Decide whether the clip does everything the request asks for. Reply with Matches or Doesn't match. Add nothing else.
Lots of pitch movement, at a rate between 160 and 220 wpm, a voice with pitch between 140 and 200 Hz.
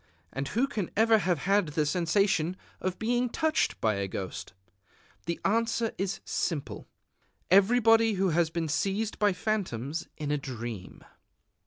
Doesn't match